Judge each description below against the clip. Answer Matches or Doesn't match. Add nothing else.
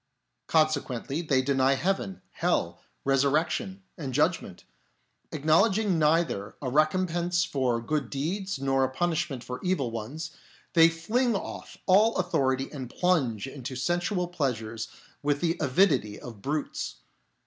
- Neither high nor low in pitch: Matches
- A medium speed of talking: Doesn't match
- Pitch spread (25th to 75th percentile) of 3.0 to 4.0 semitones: Doesn't match